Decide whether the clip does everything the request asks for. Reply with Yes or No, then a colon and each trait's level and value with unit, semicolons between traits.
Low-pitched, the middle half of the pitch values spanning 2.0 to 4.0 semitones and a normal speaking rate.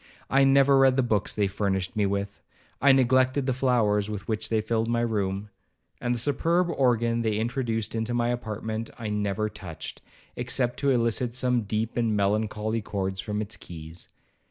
Yes: low, 110 Hz; average, 3.0 semitones; average, 165 wpm